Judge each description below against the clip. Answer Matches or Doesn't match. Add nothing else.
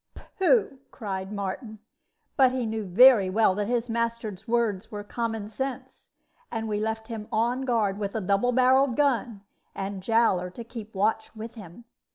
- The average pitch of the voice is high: Matches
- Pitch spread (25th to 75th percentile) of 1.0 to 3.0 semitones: Matches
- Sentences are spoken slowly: Doesn't match